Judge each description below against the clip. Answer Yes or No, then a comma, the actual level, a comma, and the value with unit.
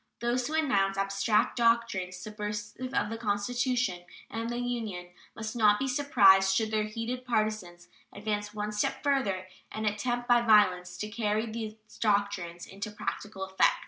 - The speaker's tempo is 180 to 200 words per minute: No, average, 150 wpm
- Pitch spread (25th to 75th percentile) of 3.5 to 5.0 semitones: No, average, 3.1 semitones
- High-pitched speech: Yes, high, 215 Hz